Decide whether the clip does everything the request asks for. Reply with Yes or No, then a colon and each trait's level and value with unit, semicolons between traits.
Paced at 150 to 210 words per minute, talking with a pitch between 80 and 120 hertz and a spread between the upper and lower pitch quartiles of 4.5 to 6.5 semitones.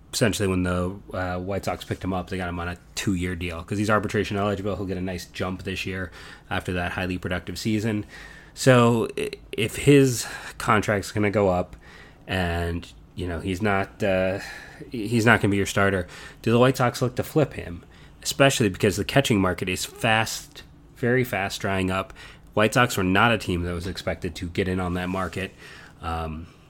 No: average, 200 wpm; very low, 95 Hz; average, 3.4 semitones